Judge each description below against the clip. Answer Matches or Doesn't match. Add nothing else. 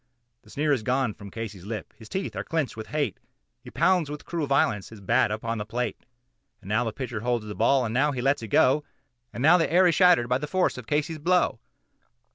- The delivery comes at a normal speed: Doesn't match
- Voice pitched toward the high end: Doesn't match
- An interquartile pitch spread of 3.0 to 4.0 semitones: Doesn't match